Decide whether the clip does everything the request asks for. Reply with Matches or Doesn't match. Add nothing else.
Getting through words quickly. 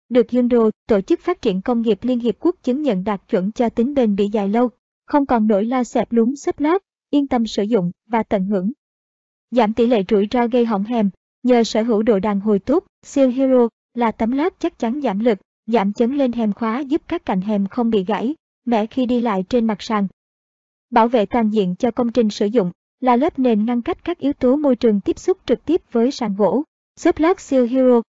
Doesn't match